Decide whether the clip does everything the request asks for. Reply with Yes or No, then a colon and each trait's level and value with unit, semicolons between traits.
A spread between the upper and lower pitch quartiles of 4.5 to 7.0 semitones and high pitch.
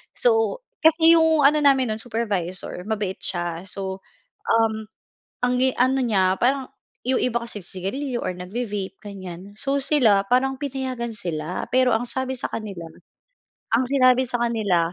Yes: average, 5.1 semitones; high, 235 Hz